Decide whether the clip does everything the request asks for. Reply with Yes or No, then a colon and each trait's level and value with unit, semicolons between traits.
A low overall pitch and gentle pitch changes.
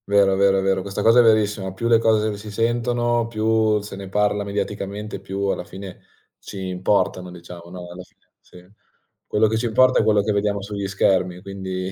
Yes: low, 100 Hz; narrow, 2.3 semitones